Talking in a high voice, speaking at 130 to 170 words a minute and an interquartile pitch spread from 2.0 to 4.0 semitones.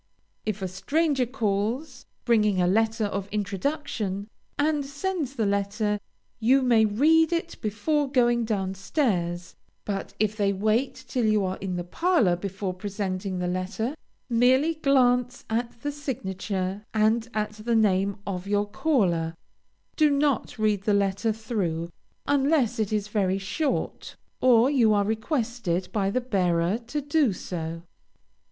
No: high, 215 Hz; average, 145 wpm; average, 4.8 semitones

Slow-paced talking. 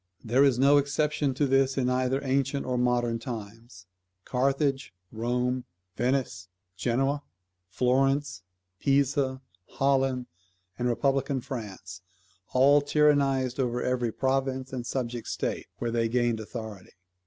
Yes: slow, 120 wpm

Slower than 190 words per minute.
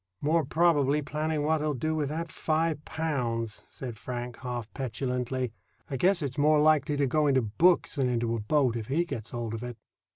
No: average, 195 wpm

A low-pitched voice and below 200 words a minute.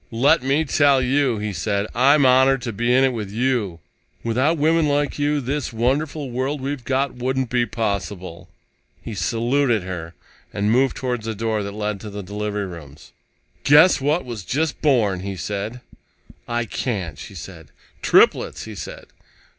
Yes: low, 120 Hz; average, 165 wpm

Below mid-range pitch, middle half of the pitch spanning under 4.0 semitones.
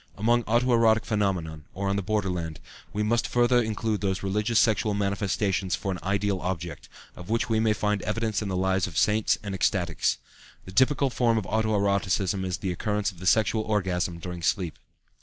Yes: low, 100 Hz; average, 2.9 semitones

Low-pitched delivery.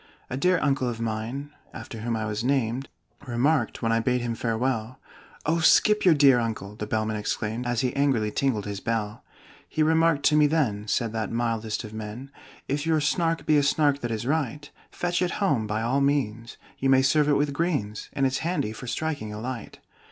Yes: low, 125 Hz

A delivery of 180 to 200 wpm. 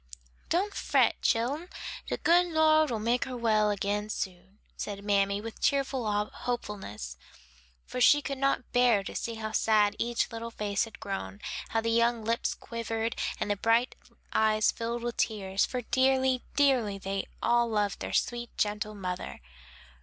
No: average, 155 wpm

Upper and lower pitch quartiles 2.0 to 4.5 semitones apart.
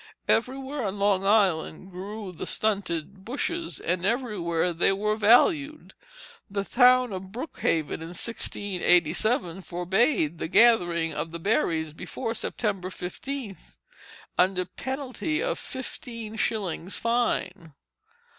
No: average, 5.0 semitones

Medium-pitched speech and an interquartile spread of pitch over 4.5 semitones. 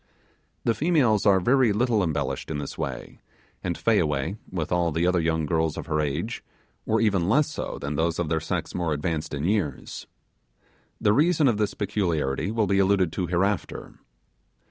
No: very low, 90 Hz; average, 5.0 semitones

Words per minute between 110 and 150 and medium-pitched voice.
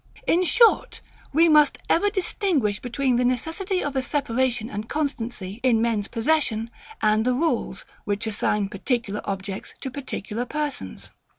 No: average, 140 wpm; high, 245 Hz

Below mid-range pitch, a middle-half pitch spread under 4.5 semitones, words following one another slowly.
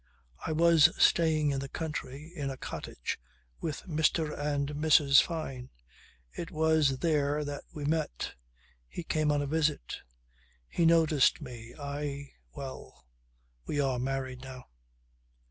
No: medium, 145 Hz; average, 2.7 semitones; slow, 130 wpm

